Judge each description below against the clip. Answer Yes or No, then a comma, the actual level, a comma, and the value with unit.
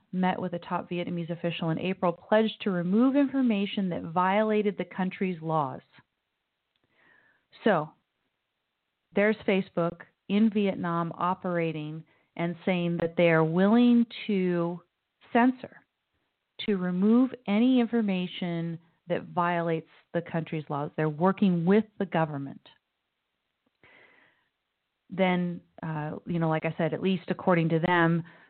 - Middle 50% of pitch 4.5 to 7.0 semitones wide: No, average, 3.3 semitones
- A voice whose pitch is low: No, medium, 180 Hz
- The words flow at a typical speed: No, slow, 120 wpm